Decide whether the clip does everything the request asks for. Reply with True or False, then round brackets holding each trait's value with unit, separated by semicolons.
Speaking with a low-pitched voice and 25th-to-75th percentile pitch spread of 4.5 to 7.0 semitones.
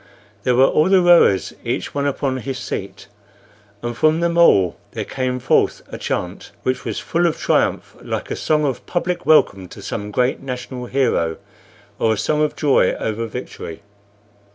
True (130 Hz; 4.8 semitones)